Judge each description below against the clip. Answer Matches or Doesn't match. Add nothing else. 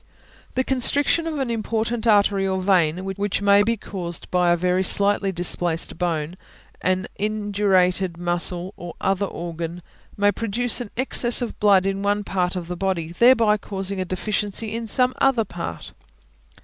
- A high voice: Matches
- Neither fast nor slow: Matches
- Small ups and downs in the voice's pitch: Doesn't match